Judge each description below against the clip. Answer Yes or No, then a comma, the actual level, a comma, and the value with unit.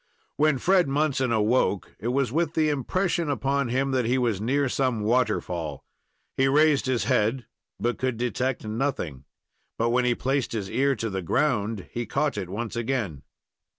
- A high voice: No, low, 125 Hz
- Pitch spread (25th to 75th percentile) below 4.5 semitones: Yes, average, 3.8 semitones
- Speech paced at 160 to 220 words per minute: Yes, average, 170 wpm